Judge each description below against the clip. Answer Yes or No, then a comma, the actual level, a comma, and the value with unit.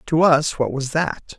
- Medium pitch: Yes, medium, 150 Hz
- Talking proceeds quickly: Yes, fast, 215 wpm